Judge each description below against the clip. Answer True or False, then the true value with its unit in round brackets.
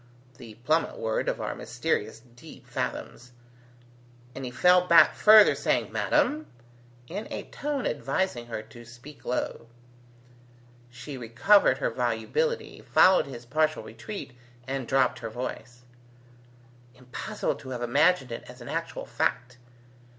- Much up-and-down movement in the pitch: True (6.9 semitones)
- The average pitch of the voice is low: True (130 Hz)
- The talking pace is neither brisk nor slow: False (130 wpm)